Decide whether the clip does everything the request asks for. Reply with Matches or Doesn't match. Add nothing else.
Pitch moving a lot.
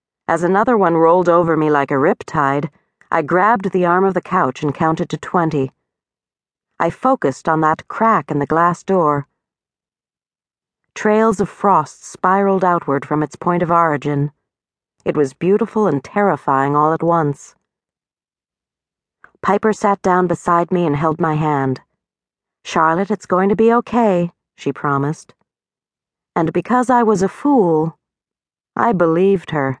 Doesn't match